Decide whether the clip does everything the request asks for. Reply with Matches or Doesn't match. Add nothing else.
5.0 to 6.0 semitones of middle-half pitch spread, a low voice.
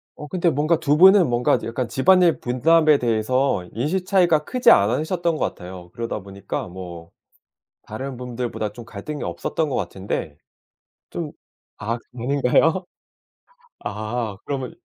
Doesn't match